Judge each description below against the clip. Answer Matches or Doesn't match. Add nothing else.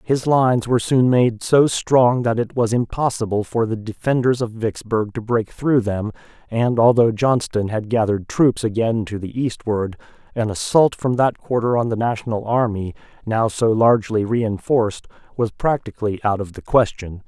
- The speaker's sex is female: Doesn't match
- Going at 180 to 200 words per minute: Doesn't match